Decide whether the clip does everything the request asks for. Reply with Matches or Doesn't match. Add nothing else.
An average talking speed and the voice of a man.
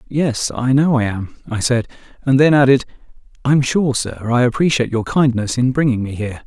Matches